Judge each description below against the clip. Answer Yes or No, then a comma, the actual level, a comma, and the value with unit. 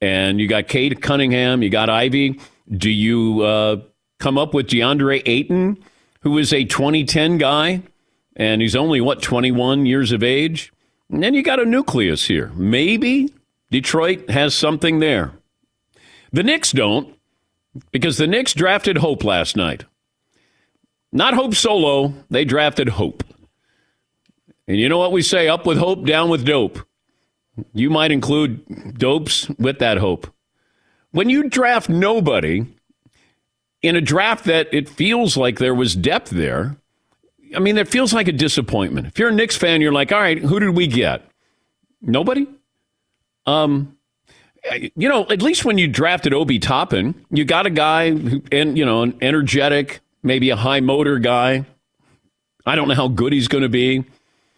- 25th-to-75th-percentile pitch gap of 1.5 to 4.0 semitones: No, wide, 5.4 semitones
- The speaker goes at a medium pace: Yes, average, 160 wpm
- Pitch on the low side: No, medium, 145 Hz